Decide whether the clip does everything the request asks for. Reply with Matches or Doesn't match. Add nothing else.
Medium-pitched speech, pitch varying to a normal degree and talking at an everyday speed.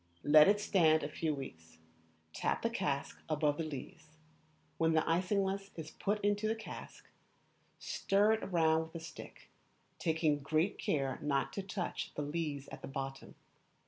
Matches